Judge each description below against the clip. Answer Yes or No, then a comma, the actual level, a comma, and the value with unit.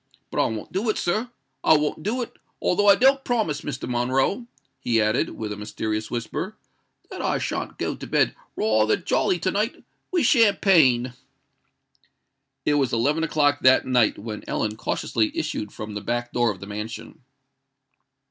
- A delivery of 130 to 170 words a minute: Yes, average, 165 wpm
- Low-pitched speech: Yes, low, 130 Hz